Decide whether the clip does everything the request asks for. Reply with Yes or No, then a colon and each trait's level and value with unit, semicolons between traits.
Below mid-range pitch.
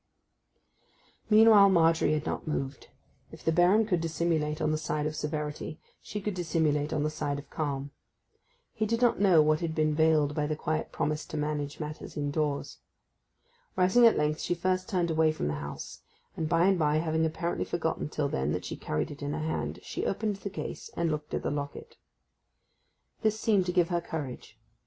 No: medium, 155 Hz